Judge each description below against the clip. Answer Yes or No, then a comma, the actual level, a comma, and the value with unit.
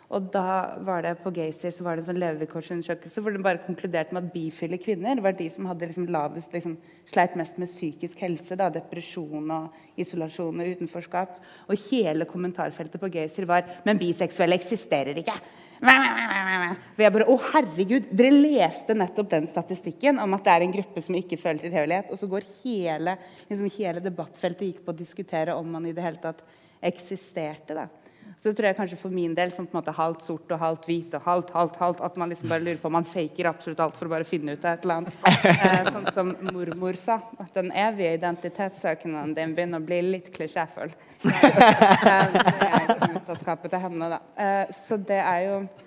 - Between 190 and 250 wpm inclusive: Yes, average, 200 wpm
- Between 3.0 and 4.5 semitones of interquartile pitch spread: No, narrow, 2.4 semitones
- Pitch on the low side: No, medium, 175 Hz